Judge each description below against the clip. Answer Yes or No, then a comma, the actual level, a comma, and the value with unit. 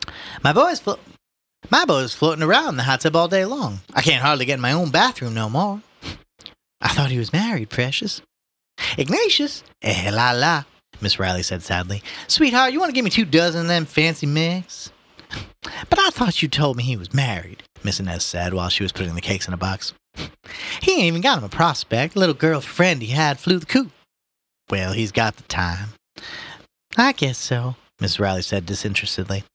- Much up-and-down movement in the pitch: Yes, wide, 9.0 semitones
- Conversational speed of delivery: Yes, average, 195 wpm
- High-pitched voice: No, low, 135 Hz